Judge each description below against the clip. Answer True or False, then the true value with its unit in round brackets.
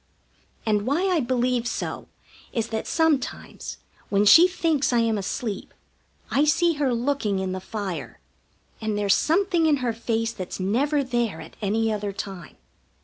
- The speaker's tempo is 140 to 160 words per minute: True (155 wpm)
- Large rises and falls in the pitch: True (5.7 semitones)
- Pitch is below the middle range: False (235 Hz)